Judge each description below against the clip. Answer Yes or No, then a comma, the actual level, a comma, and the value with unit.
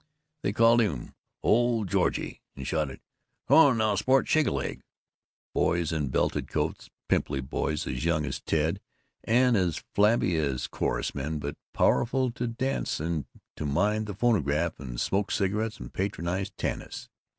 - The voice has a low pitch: Yes, very low, 95 Hz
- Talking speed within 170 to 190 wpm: No, average, 155 wpm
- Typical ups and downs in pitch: No, wide, 7.3 semitones